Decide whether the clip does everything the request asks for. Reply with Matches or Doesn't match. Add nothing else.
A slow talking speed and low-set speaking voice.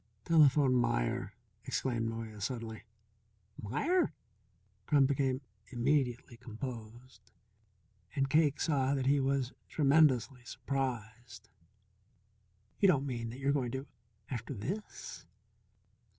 Matches